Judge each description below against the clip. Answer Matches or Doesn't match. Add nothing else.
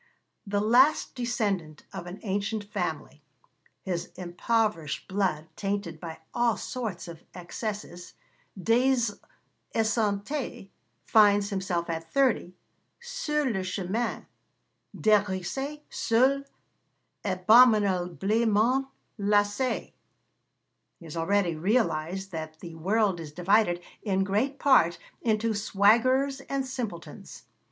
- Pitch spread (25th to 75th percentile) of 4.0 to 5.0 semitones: Matches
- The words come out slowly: Matches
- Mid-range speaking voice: Doesn't match